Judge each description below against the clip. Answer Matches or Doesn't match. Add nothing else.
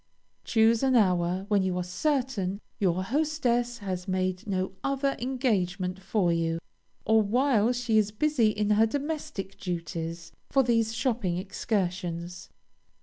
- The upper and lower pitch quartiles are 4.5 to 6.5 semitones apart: Matches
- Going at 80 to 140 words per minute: Matches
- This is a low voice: Doesn't match